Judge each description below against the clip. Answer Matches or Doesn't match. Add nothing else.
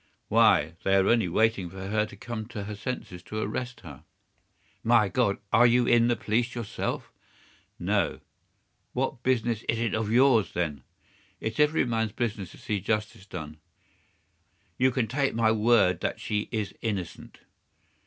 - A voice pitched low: Matches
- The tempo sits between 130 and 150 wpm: Doesn't match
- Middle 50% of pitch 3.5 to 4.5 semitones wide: Doesn't match